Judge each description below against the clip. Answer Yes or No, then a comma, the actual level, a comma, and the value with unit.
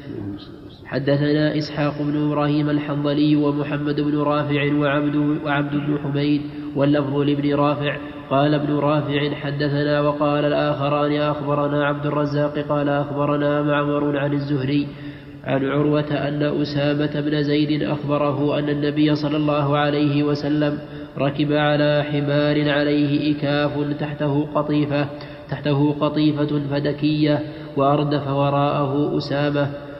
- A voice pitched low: No, medium, 145 Hz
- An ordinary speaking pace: Yes, average, 110 wpm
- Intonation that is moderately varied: No, narrow, 0.4 semitones